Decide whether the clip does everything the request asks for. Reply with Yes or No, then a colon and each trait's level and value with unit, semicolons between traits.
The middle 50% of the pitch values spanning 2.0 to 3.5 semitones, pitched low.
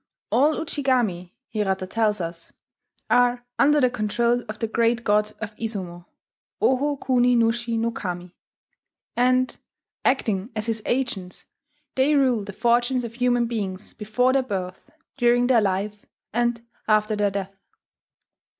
No: average, 3.2 semitones; high, 230 Hz